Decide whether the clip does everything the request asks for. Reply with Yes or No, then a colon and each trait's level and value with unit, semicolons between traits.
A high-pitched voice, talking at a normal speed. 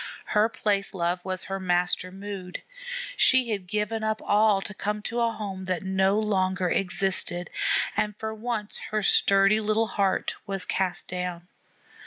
Yes: high, 195 Hz; average, 155 wpm